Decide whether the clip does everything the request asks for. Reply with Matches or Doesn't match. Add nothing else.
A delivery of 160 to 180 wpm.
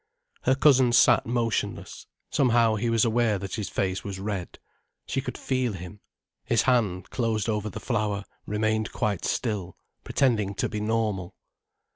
Doesn't match